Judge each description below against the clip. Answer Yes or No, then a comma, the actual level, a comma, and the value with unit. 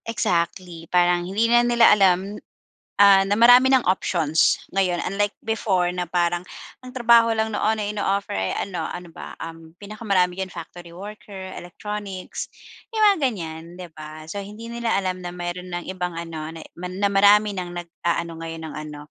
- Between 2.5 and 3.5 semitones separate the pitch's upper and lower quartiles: Yes, average, 3.2 semitones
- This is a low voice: No, medium, 185 Hz